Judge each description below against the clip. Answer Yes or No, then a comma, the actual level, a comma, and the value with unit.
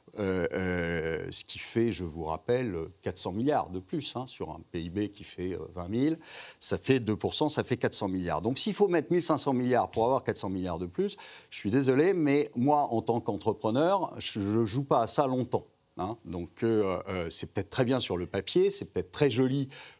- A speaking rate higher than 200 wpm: Yes, average, 215 wpm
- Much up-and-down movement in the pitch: Yes, wide, 6.7 semitones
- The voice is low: Yes, low, 115 Hz